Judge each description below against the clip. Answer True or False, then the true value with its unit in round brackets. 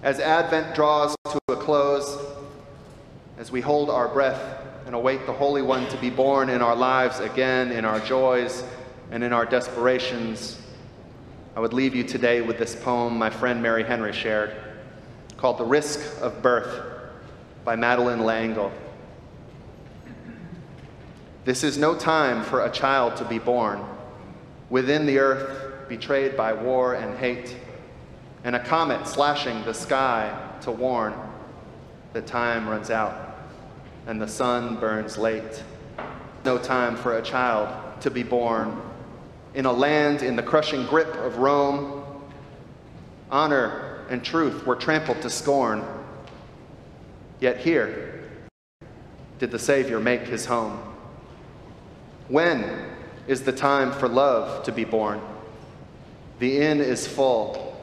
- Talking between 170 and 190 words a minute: False (135 wpm)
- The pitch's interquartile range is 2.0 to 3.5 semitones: True (3.1 semitones)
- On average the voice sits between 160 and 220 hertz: False (125 Hz)